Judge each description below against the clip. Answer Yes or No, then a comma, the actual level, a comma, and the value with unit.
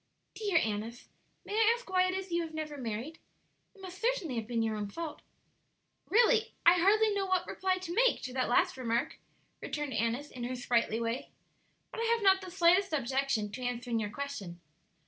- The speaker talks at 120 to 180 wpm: No, average, 195 wpm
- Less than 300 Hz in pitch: No, very high, 310 Hz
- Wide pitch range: Yes, wide, 8.1 semitones